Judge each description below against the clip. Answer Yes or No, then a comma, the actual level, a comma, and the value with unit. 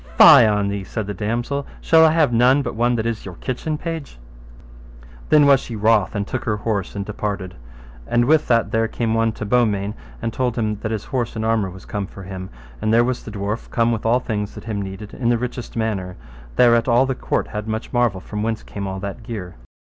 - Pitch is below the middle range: Yes, low, 110 Hz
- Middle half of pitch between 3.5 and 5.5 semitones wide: No, average, 2.9 semitones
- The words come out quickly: Yes, fast, 225 wpm